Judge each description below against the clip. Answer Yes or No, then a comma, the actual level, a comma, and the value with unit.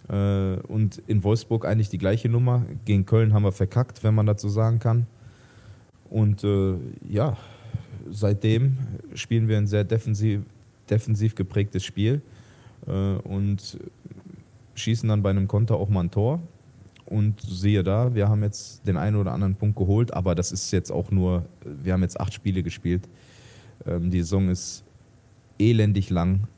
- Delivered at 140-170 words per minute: Yes, average, 155 wpm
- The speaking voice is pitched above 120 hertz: No, low, 105 Hz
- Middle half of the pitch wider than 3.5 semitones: No, average, 2.8 semitones